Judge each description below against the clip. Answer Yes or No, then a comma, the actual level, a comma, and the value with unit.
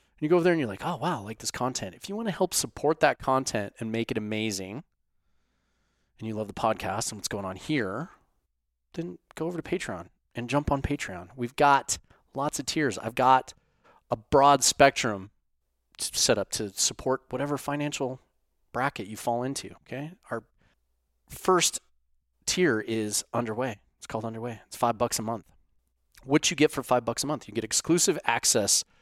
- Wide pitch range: Yes, wide, 7.0 semitones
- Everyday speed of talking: Yes, average, 190 wpm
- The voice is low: Yes, low, 120 Hz